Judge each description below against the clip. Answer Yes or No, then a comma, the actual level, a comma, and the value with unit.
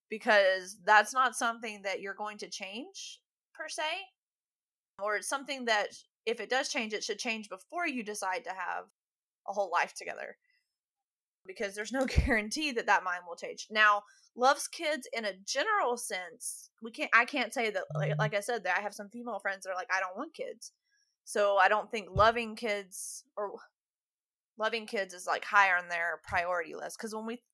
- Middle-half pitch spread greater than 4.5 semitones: Yes, average, 5.1 semitones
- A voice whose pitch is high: Yes, high, 220 Hz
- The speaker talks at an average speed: Yes, average, 195 wpm